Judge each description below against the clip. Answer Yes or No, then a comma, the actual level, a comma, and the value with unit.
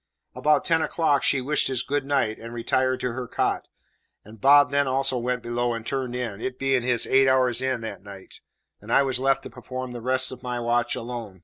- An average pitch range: No, narrow, 2.2 semitones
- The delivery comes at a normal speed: No, fast, 220 wpm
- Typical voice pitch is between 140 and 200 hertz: No, low, 125 Hz